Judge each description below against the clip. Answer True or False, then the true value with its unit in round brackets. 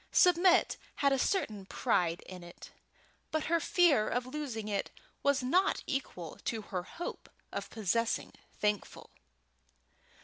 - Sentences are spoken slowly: True (130 wpm)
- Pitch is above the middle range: True (245 Hz)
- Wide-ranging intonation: True (6.8 semitones)